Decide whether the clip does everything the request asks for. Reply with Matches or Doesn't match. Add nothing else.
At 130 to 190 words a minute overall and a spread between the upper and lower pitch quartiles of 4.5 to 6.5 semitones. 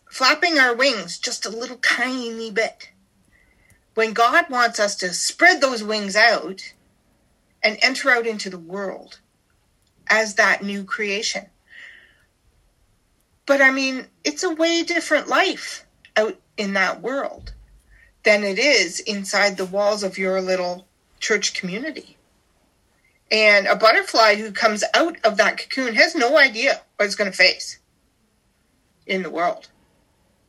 Matches